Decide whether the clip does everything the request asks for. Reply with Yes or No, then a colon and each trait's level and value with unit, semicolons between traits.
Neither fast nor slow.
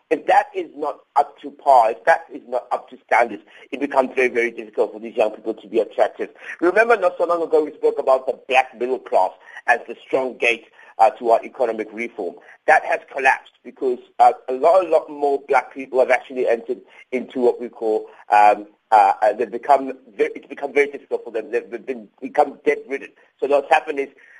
No: fast, 210 wpm